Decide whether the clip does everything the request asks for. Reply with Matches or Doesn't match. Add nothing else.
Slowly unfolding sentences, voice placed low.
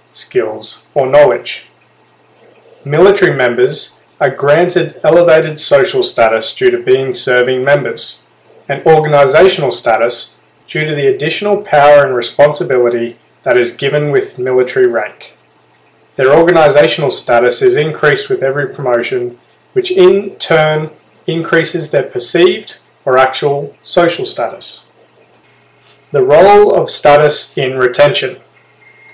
Doesn't match